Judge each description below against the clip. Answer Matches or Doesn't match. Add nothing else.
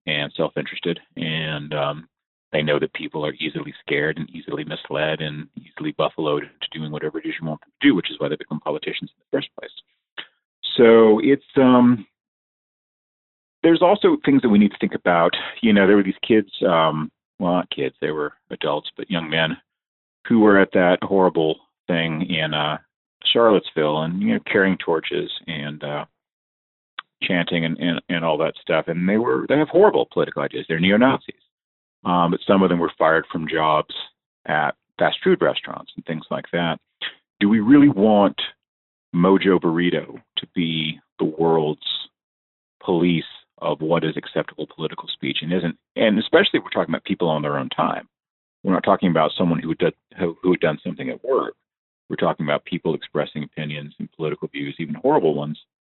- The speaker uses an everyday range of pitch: Matches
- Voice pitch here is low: Matches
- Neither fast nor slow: Matches